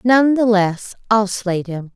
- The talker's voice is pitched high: Yes, high, 210 Hz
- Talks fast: No, average, 185 wpm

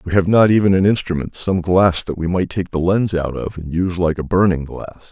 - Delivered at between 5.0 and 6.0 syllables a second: Yes, 5.4 syllables/s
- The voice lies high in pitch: No, very low, 90 Hz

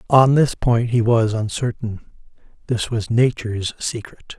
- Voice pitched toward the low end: Yes, low, 115 Hz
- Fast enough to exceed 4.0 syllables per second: Yes, 4.3 syllables/s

